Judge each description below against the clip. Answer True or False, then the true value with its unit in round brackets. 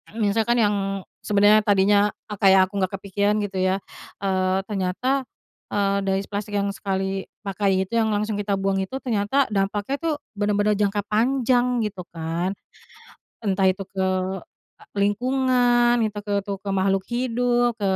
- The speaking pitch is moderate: False (205 Hz)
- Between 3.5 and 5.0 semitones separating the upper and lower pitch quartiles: False (2.7 semitones)